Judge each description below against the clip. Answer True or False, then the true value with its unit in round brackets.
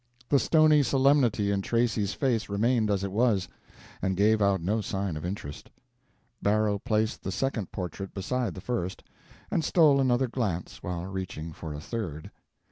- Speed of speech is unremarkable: True (160 wpm)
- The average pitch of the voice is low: True (105 Hz)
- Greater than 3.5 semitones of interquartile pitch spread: True (4.4 semitones)